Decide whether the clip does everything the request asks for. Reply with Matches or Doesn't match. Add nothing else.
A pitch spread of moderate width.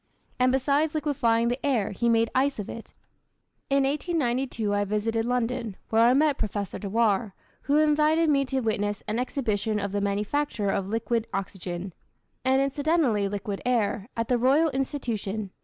Matches